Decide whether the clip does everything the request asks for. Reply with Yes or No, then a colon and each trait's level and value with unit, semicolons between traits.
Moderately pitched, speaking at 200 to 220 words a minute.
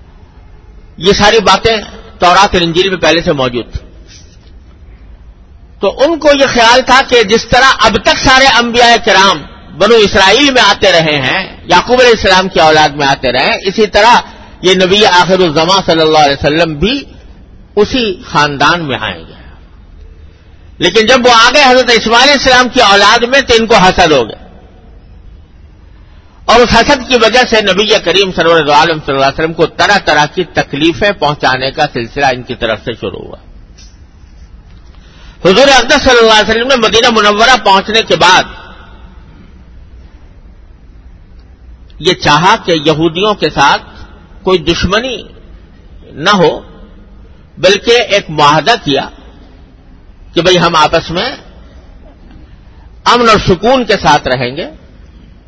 No: medium, 160 Hz; average, 145 wpm